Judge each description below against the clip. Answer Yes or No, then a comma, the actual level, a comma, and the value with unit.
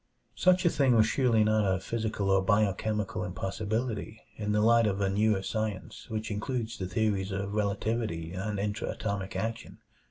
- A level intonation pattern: Yes, narrow, 2.2 semitones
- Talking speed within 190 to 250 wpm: No, average, 165 wpm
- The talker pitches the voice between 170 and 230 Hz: No, low, 105 Hz